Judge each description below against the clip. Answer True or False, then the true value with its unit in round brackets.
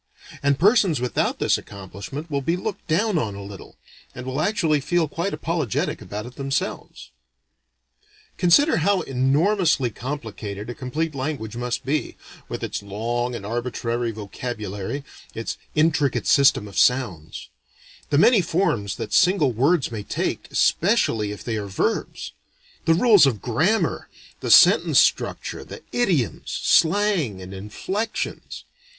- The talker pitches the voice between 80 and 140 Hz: True (135 Hz)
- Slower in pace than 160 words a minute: True (135 wpm)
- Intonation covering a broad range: True (7.0 semitones)